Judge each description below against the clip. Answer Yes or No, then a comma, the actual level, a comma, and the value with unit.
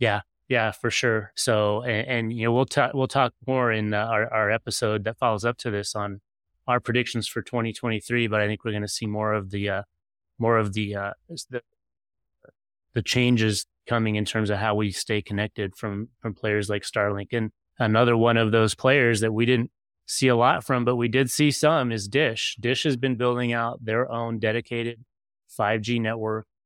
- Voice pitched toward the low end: Yes, low, 115 Hz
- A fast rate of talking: Yes, fast, 210 wpm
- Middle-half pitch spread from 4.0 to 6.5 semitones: No, narrow, 2.5 semitones